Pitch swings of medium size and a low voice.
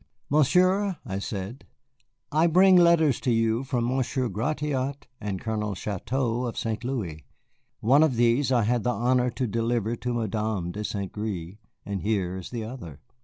Yes: average, 4.1 semitones; low, 120 Hz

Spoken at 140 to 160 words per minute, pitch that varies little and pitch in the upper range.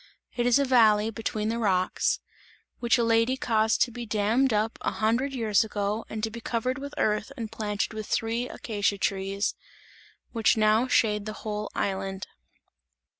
No: average, 170 wpm; narrow, 2.0 semitones; high, 220 Hz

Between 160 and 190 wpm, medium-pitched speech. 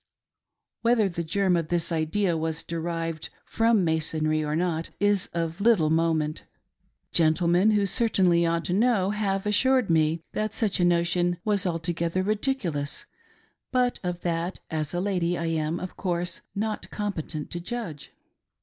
No: average, 150 wpm; medium, 175 Hz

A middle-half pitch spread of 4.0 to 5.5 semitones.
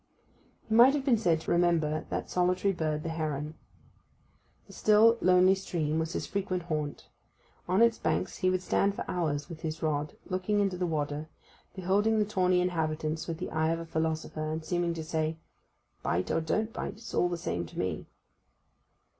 No: average, 3.2 semitones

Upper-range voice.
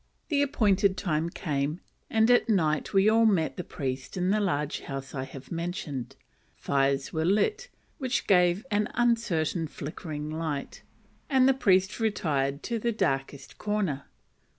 No: medium, 175 Hz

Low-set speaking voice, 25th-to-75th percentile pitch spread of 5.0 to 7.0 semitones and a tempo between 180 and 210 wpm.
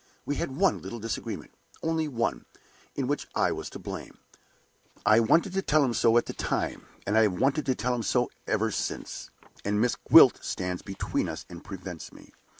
Yes: low, 115 Hz; average, 5.3 semitones; average, 195 wpm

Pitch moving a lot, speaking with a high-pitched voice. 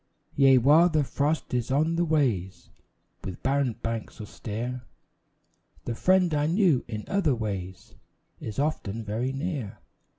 No: wide, 5.7 semitones; low, 135 Hz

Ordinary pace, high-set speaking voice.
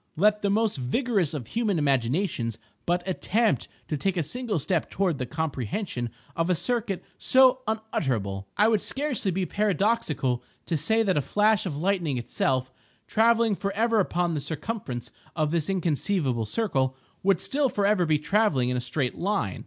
No: average, 160 wpm; medium, 180 Hz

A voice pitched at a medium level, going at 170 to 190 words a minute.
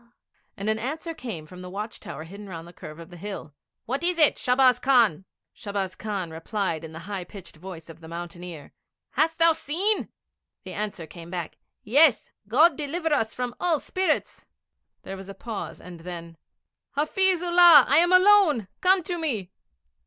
No: high, 215 Hz; average, 180 wpm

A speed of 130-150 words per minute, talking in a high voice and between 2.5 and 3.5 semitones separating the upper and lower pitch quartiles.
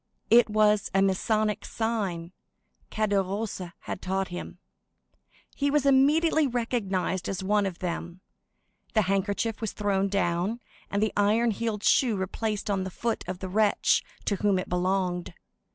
Yes: average, 145 wpm; high, 200 Hz; average, 2.8 semitones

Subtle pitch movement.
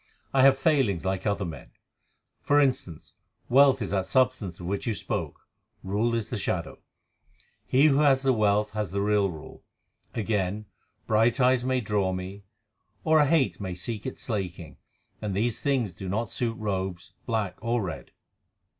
No: average, 5.0 semitones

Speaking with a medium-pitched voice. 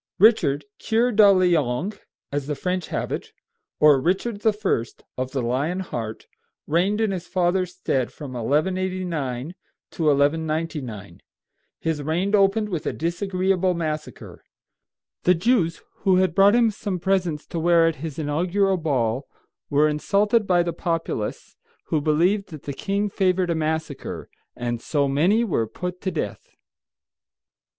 Yes: medium, 170 Hz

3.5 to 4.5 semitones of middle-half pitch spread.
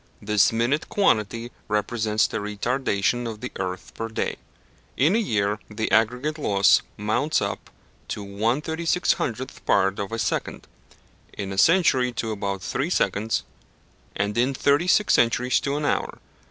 No: average, 4.9 semitones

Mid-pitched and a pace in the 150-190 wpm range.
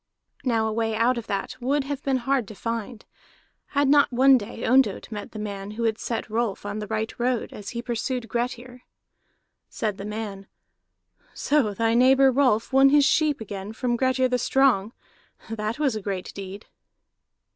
No: high, 235 Hz; average, 180 wpm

